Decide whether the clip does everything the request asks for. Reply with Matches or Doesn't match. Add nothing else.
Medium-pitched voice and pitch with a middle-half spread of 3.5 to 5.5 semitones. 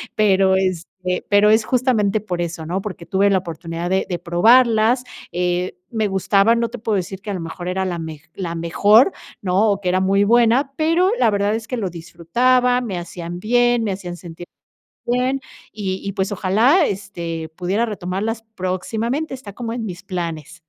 Doesn't match